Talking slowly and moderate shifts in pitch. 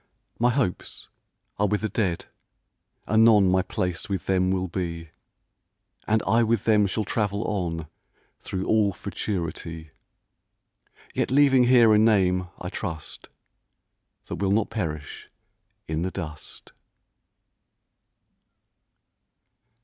Yes: slow, 110 wpm; average, 3.6 semitones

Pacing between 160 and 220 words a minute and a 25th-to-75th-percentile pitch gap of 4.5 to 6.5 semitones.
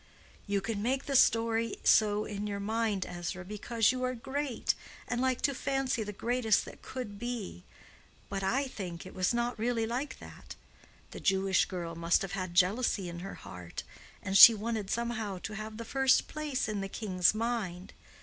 No: average, 180 wpm; average, 4.0 semitones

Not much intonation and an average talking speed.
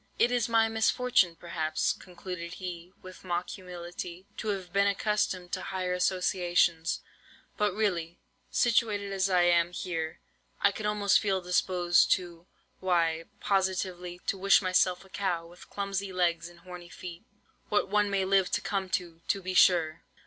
Yes: narrow, 2.2 semitones; average, 155 wpm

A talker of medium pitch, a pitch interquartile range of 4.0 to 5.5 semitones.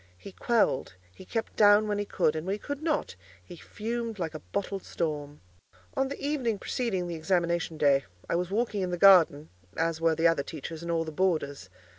Yes: medium, 175 Hz; average, 4.7 semitones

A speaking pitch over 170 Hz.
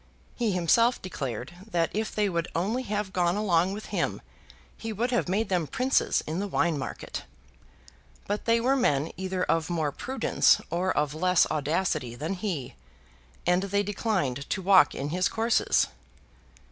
Yes: medium, 185 Hz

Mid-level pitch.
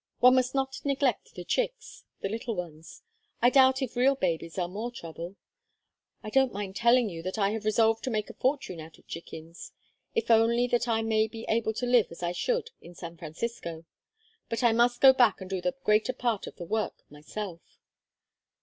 No: high, 225 Hz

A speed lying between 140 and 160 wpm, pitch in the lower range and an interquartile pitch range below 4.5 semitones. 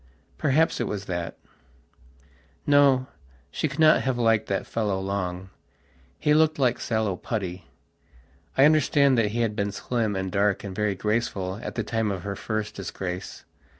No: average, 155 wpm; low, 105 Hz; average, 4.9 semitones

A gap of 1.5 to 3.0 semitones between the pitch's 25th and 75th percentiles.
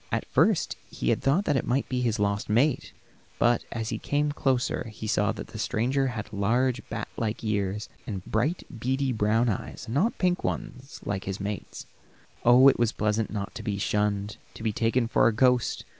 No: average, 3.5 semitones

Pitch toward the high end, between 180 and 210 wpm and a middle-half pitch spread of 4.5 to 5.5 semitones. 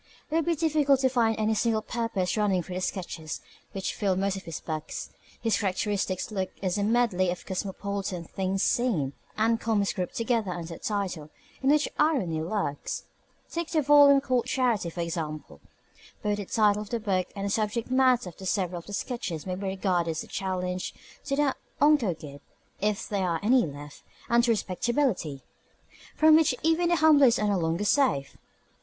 Yes: high, 205 Hz; average, 185 wpm; average, 5.1 semitones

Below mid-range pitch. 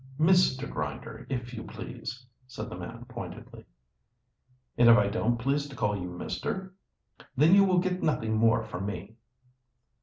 Yes: low, 120 Hz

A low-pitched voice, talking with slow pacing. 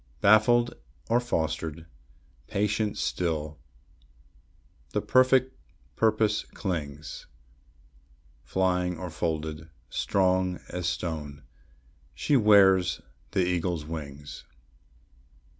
Yes: very low, 90 Hz; slow, 75 wpm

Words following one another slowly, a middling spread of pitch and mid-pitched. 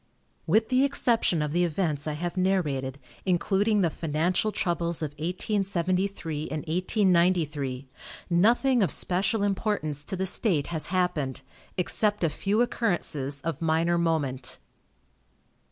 Yes: slow, 125 wpm; average, 4.2 semitones; medium, 175 Hz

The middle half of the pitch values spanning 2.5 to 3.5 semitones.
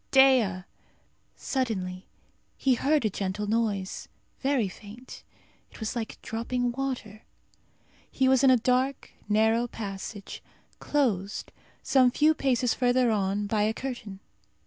No: average, 3.9 semitones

